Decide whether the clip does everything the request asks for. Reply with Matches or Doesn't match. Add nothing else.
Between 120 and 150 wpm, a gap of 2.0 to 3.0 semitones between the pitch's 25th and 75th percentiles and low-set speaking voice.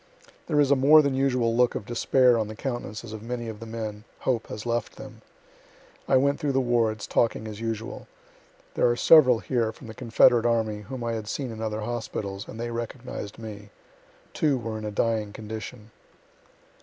Doesn't match